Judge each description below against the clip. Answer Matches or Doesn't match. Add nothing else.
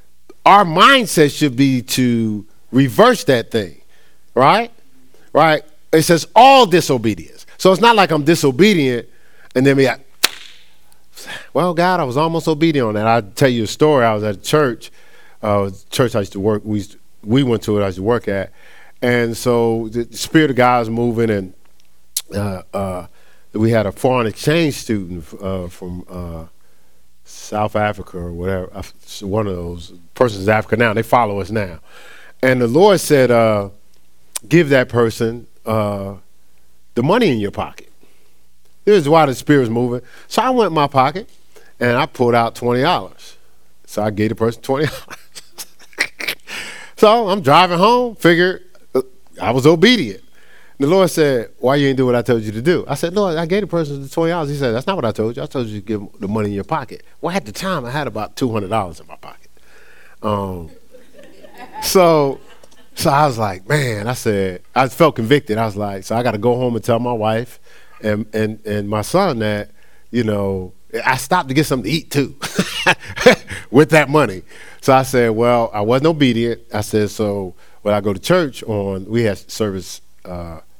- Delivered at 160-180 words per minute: Doesn't match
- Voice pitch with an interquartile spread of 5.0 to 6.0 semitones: Matches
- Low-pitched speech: Matches